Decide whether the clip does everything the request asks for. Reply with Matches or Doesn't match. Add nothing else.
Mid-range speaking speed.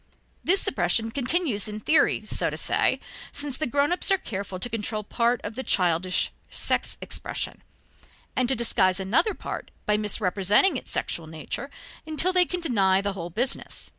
Matches